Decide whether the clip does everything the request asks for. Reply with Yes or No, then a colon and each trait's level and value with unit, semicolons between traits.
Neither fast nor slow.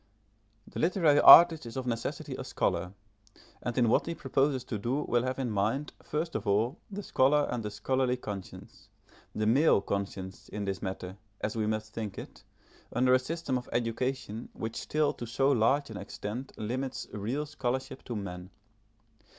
Yes: average, 175 wpm